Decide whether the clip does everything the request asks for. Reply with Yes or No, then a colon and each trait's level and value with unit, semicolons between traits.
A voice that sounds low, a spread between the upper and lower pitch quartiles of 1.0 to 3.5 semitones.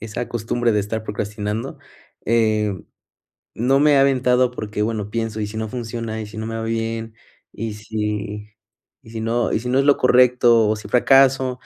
Yes: low, 115 Hz; narrow, 2.5 semitones